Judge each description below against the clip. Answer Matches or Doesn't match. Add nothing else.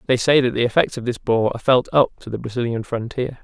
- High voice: Doesn't match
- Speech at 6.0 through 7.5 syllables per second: Matches